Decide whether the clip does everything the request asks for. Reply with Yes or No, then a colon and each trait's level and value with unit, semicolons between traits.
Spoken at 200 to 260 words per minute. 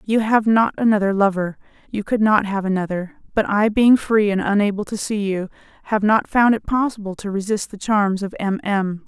Yes: fast, 205 wpm